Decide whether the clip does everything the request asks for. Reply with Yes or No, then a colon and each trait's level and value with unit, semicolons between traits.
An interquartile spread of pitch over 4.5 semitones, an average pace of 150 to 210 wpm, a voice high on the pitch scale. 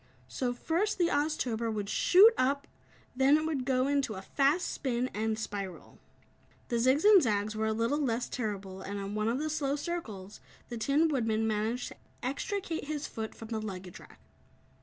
Yes: average, 5.2 semitones; average, 180 wpm; high, 245 Hz